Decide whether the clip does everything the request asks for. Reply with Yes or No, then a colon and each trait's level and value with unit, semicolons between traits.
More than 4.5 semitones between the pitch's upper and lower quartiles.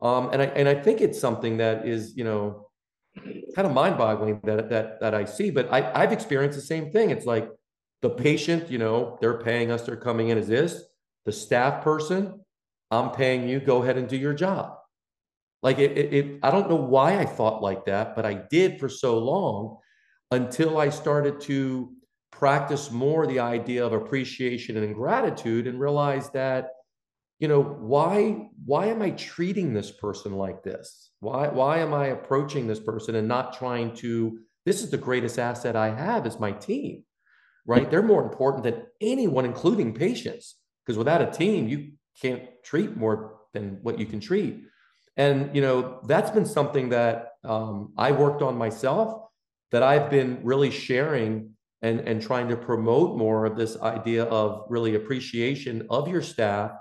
No: average, 4.0 semitones